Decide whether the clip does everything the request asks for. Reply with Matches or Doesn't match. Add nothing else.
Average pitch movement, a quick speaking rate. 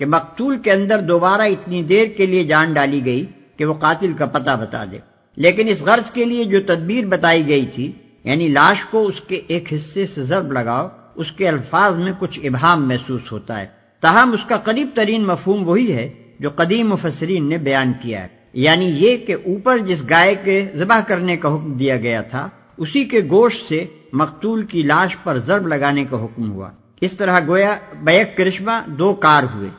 Doesn't match